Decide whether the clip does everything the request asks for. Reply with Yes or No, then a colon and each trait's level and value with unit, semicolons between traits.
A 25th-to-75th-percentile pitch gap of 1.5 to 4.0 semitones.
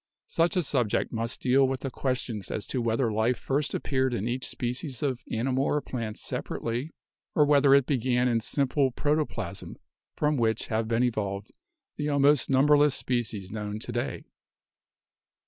Yes: average, 3.5 semitones